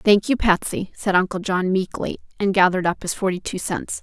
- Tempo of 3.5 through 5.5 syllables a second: Yes, 5.4 syllables/s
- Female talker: Yes, female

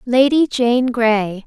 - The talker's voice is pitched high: Yes, high, 240 Hz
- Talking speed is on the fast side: No, slow, 125 wpm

